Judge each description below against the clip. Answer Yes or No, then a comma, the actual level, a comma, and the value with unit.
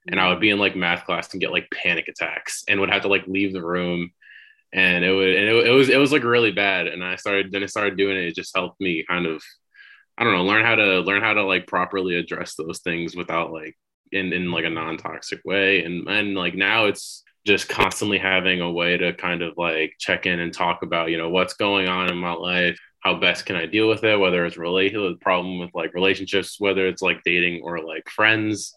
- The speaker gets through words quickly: Yes, fast, 245 wpm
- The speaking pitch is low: Yes, very low, 95 Hz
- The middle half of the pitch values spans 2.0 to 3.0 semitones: Yes, narrow, 2.4 semitones